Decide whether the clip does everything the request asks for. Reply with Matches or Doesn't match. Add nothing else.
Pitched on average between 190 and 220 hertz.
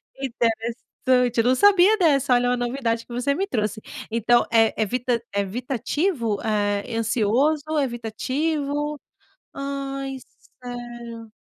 Doesn't match